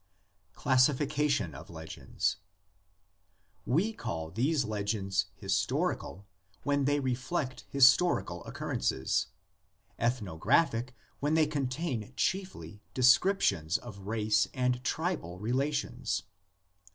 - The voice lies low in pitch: Yes, low, 125 Hz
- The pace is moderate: No, slow, 85 wpm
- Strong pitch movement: Yes, wide, 6.1 semitones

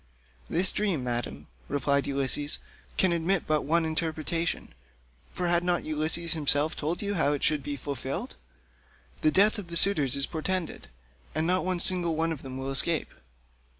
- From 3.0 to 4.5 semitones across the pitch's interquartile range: Yes, average, 3.6 semitones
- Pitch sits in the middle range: Yes, medium, 160 Hz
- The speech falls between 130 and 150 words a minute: No, average, 170 wpm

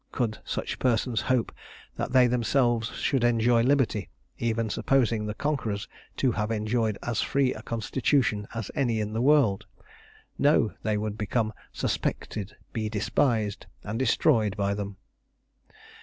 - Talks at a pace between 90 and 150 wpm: Yes, average, 140 wpm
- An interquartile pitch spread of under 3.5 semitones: Yes, average, 2.8 semitones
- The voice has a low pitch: Yes, low, 115 Hz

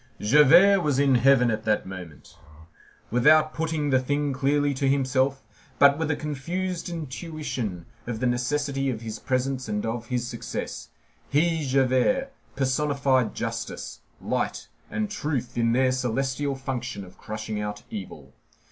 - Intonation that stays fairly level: No, average, 3.4 semitones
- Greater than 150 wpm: No, average, 140 wpm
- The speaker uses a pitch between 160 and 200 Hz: No, low, 135 Hz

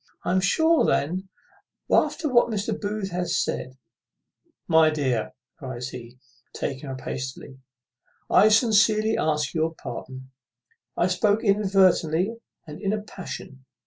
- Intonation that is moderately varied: No, wide, 7.7 semitones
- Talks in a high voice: No, medium, 180 Hz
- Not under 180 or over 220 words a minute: No, slow, 135 wpm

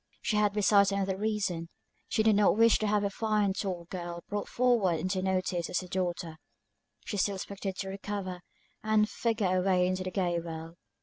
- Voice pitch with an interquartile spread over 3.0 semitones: No, narrow, 2.5 semitones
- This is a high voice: Yes, high, 195 Hz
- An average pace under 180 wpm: No, average, 185 wpm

